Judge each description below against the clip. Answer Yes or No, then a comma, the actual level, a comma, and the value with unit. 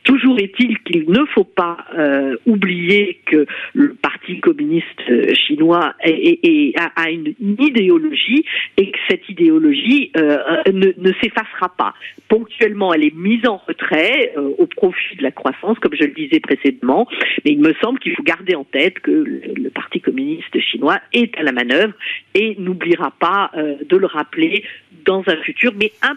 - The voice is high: Yes, high, 225 Hz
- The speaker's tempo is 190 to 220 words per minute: No, average, 175 wpm